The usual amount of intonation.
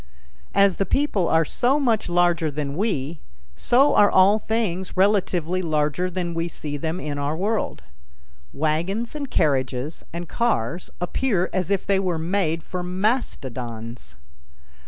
Yes: average, 4.7 semitones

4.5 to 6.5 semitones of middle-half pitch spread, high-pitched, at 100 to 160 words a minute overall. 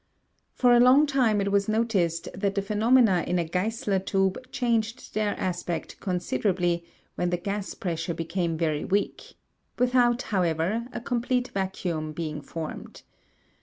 Yes: average, 4.9 semitones; high, 195 Hz; average, 140 wpm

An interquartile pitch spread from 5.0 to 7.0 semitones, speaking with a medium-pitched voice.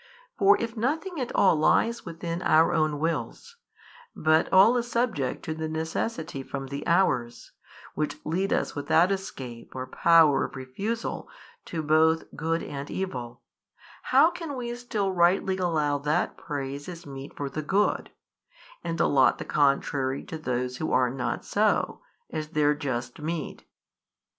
Yes: average, 5.3 semitones; medium, 160 Hz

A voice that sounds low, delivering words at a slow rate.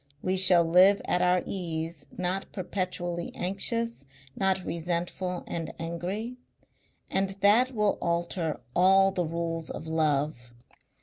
No: medium, 180 Hz; slow, 120 wpm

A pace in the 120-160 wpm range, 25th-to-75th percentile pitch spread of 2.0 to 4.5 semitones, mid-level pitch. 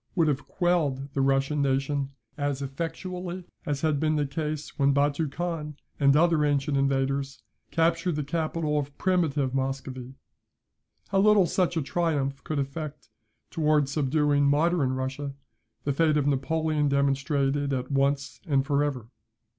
Yes: average, 145 wpm; narrow, 2.5 semitones; medium, 145 Hz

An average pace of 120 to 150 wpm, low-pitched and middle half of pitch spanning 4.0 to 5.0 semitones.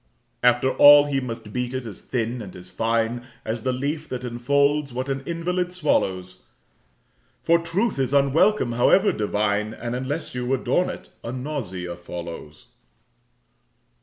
Yes: average, 145 wpm; low, 125 Hz; average, 4.3 semitones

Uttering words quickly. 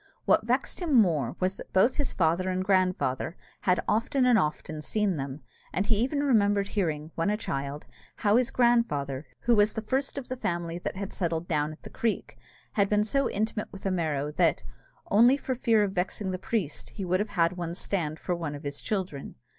Yes: fast, 210 wpm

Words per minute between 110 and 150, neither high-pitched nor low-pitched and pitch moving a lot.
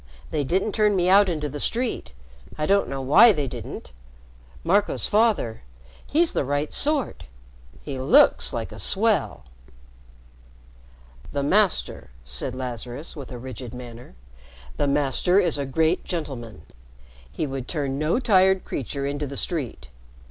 Yes: average, 140 wpm; medium, 145 Hz; wide, 6.6 semitones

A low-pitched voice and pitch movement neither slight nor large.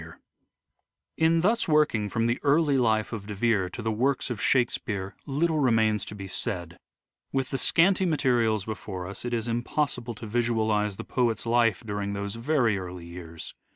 Yes: low, 115 Hz; average, 4.4 semitones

